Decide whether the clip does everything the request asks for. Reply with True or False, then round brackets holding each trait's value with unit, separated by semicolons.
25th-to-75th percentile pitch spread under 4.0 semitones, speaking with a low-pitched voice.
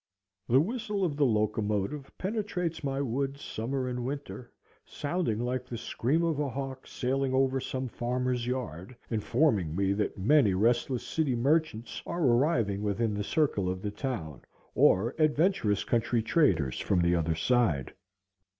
False (5.0 semitones; 125 Hz)